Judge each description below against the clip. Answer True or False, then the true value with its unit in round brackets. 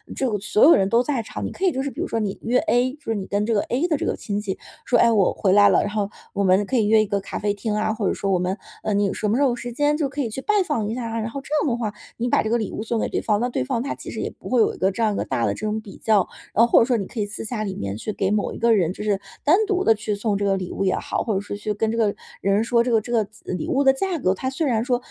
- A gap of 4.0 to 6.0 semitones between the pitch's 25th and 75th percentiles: False (3.2 semitones)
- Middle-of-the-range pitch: False (220 Hz)